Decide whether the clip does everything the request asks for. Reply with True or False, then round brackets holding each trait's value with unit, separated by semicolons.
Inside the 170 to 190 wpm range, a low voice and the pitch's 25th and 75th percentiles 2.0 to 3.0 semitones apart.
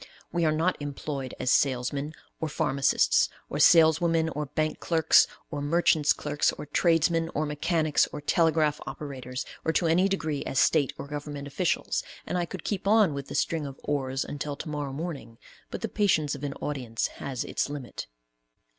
False (175 wpm; 150 Hz; 2.7 semitones)